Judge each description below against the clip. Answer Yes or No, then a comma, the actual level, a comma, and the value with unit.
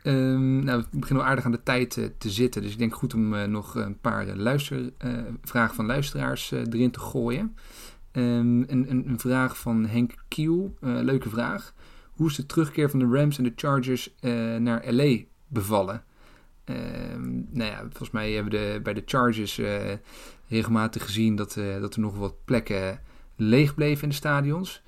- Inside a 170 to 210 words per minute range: Yes, average, 195 wpm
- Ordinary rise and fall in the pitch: Yes, average, 3.3 semitones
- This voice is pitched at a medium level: No, low, 120 Hz